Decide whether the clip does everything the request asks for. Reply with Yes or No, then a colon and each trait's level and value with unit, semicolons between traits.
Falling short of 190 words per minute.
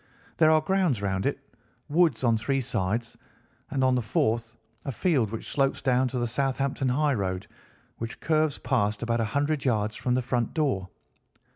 Yes: average, 170 wpm